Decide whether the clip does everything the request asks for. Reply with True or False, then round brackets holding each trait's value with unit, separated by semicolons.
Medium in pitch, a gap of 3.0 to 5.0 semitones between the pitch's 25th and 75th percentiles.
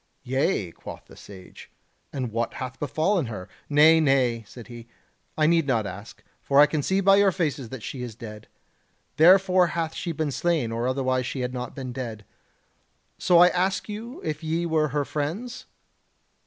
False (145 Hz; 5.4 semitones)